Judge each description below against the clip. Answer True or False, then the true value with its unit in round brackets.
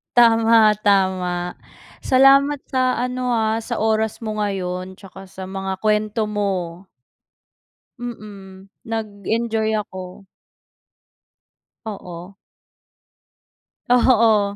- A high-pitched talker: True (210 Hz)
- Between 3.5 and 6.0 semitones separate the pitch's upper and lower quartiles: False (2.9 semitones)